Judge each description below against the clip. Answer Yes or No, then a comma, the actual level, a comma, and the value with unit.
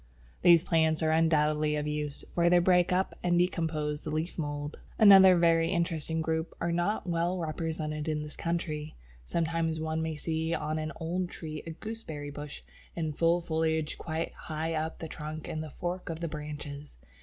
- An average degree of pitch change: No, narrow, 1.8 semitones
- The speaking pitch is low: No, medium, 160 Hz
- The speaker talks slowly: No, average, 180 wpm